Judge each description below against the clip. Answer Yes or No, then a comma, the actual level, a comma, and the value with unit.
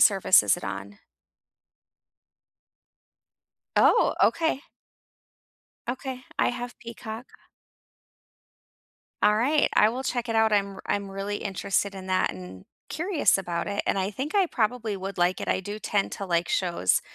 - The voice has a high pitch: Yes, high, 205 Hz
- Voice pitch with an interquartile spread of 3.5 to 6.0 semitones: Yes, average, 4.4 semitones